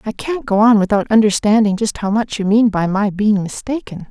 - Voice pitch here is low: No, high, 215 Hz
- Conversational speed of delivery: No, fast, 220 wpm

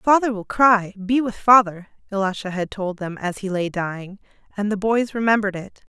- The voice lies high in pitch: Yes, high, 205 Hz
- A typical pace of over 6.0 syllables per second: No, 5.2 syllables/s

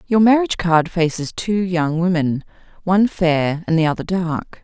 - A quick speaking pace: No, average, 170 wpm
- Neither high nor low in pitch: Yes, medium, 175 Hz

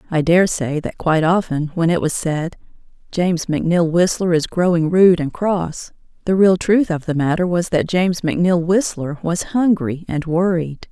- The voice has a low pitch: No, medium, 170 Hz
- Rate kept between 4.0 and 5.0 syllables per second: Yes, 4.8 syllables/s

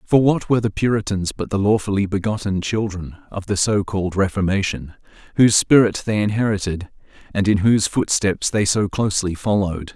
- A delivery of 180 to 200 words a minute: No, average, 165 wpm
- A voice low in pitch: Yes, low, 100 Hz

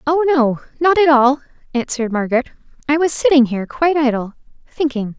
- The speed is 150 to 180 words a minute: Yes, average, 160 wpm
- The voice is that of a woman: Yes, female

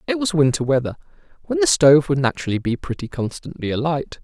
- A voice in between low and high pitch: Yes, medium, 155 Hz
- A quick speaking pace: No, average, 185 wpm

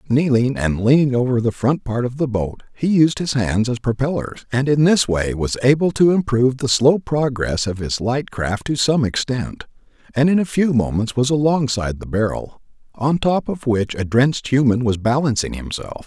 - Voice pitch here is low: Yes, low, 125 Hz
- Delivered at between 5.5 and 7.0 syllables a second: No, 4.9 syllables/s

